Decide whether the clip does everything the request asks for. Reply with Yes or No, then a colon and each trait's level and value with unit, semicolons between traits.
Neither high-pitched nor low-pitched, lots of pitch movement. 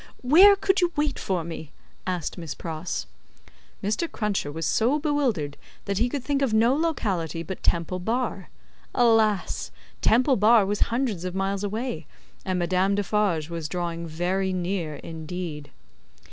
No: high, 195 Hz; wide, 5.9 semitones